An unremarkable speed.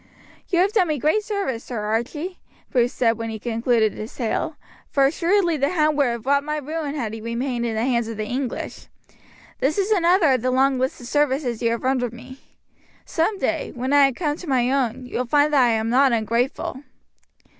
No: fast, 210 wpm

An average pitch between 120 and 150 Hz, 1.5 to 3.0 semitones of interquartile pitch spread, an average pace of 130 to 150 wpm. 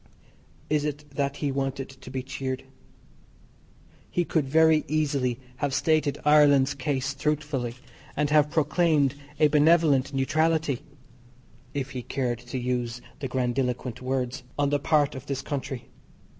Yes: medium, 140 Hz; narrow, 2.4 semitones; slow, 135 wpm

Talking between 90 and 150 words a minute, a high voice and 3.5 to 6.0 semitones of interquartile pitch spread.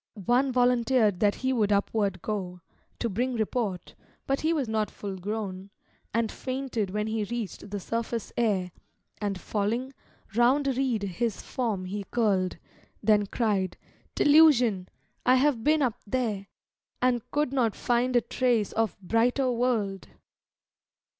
Yes: average, 140 wpm; high, 225 Hz; average, 3.8 semitones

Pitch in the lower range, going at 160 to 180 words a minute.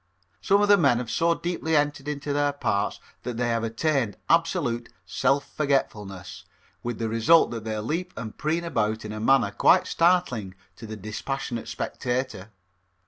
Yes: low, 125 Hz; average, 165 wpm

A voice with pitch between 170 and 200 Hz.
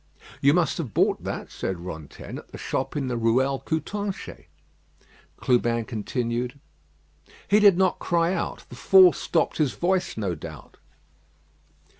No: low, 135 Hz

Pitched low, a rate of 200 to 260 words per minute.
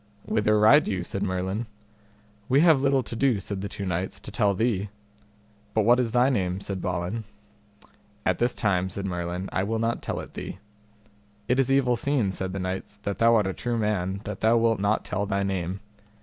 Yes: low, 105 Hz; fast, 205 wpm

